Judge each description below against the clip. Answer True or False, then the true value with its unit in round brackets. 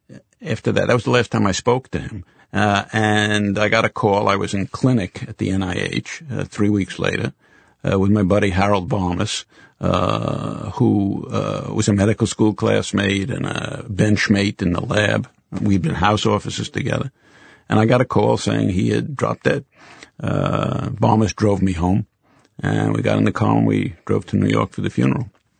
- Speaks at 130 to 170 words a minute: False (195 wpm)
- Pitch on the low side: True (105 Hz)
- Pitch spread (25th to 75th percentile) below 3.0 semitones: True (2.5 semitones)